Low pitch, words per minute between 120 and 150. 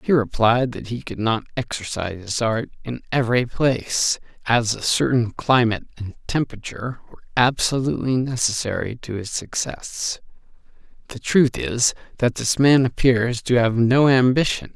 Yes: low, 120 Hz; average, 140 wpm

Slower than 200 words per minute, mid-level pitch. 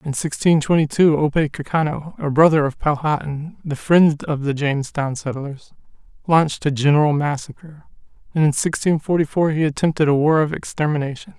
Yes: average, 160 wpm; medium, 150 Hz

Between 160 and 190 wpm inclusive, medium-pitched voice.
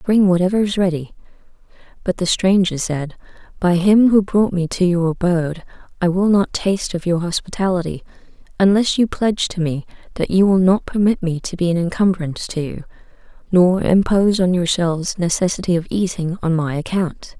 Yes: average, 170 wpm; medium, 180 Hz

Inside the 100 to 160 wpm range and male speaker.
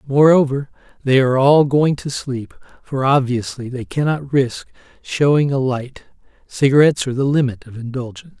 Yes: average, 150 wpm; male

